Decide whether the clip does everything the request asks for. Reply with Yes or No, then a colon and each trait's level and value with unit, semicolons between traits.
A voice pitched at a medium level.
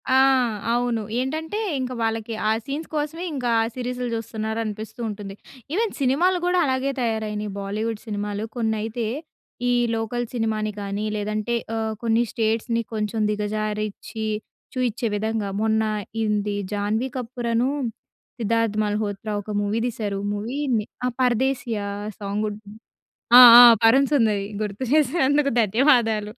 No: high, 225 Hz